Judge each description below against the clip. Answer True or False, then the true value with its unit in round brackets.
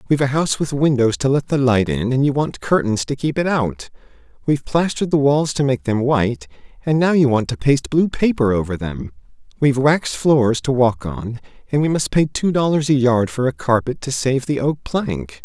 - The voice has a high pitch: False (130 Hz)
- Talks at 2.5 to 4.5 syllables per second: False (5.4 syllables/s)